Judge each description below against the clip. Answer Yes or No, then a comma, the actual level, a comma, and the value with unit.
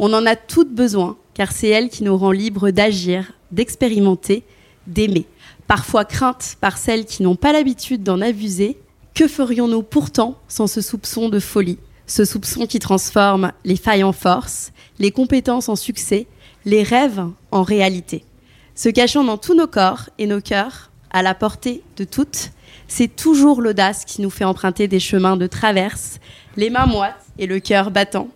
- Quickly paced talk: No, average, 170 wpm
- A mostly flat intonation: No, average, 3.7 semitones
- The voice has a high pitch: Yes, high, 205 Hz